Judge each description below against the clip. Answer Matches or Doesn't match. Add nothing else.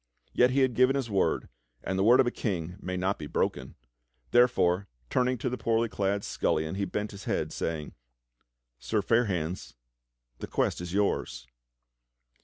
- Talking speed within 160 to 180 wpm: Matches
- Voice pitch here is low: Matches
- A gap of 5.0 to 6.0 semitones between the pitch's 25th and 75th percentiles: Matches